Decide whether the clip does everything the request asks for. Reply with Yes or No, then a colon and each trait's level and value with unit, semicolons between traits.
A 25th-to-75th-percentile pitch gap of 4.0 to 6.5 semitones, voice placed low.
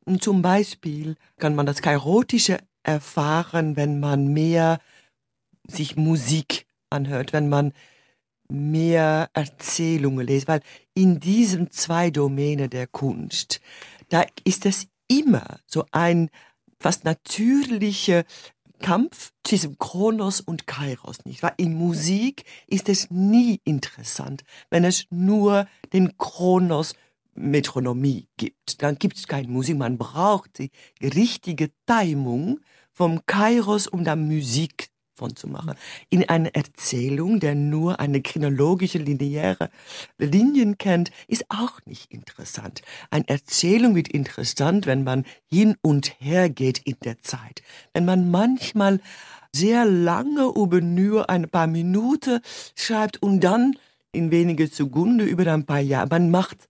No: average, 5.1 semitones; medium, 165 Hz